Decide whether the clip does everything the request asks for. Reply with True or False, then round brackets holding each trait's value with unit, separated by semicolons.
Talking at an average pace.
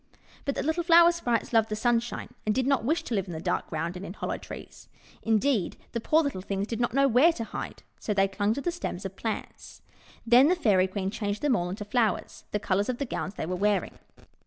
False (245 wpm)